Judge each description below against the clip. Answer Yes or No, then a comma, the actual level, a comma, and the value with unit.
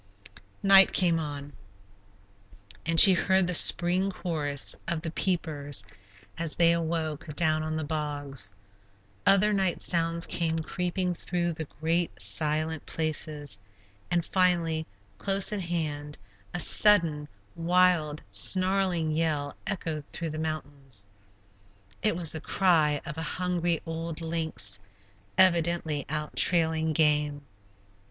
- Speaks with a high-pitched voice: No, medium, 160 Hz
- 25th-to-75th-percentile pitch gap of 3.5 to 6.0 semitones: No, narrow, 2.6 semitones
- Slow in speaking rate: Yes, slow, 120 wpm